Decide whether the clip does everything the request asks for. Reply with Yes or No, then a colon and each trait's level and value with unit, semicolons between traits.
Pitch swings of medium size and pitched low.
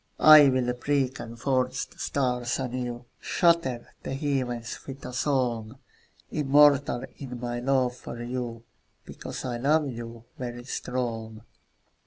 No: narrow, 2.3 semitones; low, 125 Hz